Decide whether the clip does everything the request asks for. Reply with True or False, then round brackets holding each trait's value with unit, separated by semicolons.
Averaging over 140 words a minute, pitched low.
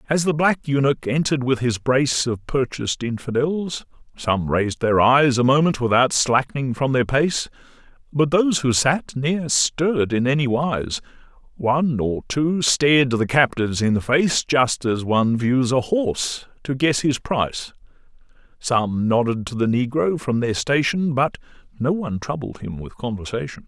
True (160 wpm; 130 Hz)